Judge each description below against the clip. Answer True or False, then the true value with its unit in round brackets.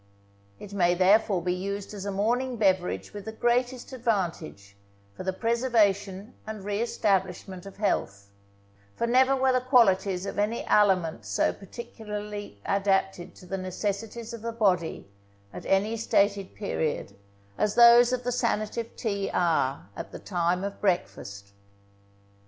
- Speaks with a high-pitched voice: True (200 Hz)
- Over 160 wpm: False (145 wpm)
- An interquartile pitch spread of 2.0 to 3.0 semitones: False (3.7 semitones)